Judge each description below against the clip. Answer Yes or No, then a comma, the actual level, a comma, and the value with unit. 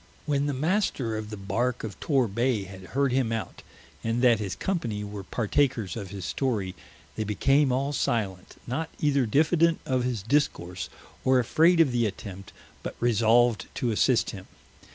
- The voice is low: Yes, low, 120 Hz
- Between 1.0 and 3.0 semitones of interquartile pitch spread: No, average, 4.8 semitones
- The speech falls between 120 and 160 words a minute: No, average, 170 wpm